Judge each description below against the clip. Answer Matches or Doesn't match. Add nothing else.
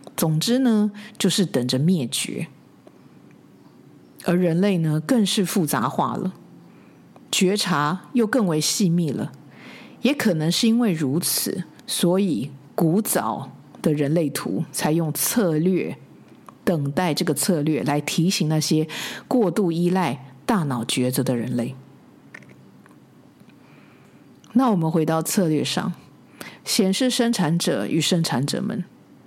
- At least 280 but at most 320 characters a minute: Doesn't match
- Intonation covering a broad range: Doesn't match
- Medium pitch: Matches